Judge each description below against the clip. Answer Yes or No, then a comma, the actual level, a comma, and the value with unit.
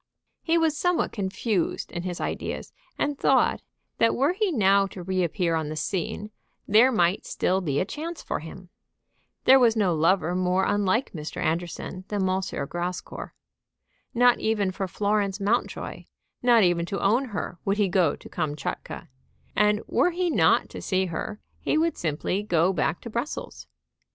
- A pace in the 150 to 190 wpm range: Yes, average, 165 wpm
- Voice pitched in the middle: No, high, 195 Hz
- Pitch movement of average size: Yes, average, 4.6 semitones